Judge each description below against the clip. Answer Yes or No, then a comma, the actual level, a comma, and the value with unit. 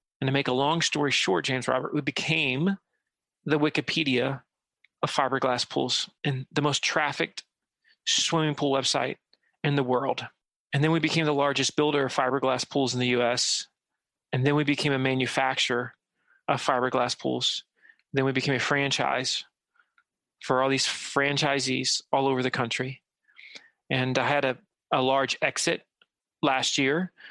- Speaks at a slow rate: No, average, 155 wpm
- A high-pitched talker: No, medium, 140 Hz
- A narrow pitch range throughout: Yes, narrow, 2.2 semitones